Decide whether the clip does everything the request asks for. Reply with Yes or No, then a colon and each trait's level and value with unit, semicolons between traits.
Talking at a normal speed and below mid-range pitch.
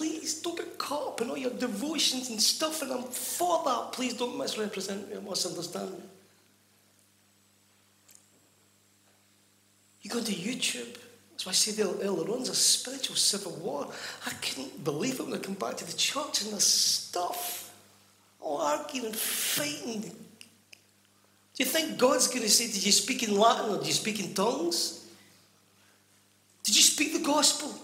No: average, 170 wpm; high, 210 Hz